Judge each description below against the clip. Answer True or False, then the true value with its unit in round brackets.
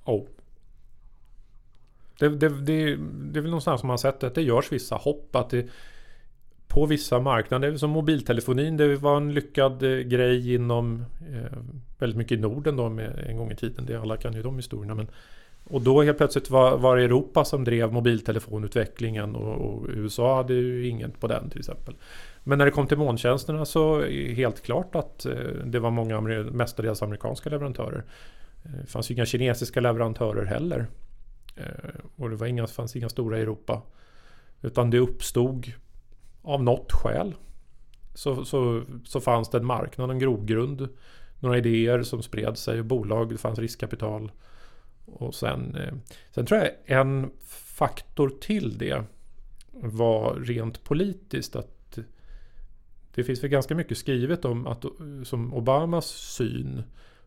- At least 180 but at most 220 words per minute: False (160 wpm)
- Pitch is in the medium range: False (125 Hz)